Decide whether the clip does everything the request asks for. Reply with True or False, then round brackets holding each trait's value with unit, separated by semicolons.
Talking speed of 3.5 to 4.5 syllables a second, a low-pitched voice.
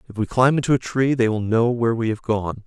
False (6.0 syllables/s; 115 Hz)